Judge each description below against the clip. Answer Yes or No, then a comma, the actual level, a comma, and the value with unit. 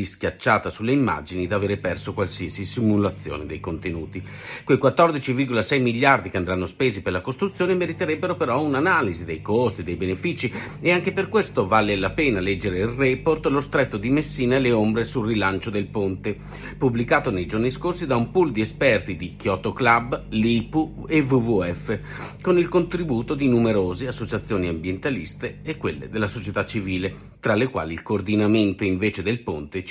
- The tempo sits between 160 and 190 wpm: Yes, average, 165 wpm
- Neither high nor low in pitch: No, low, 115 Hz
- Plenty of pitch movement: Yes, wide, 5.9 semitones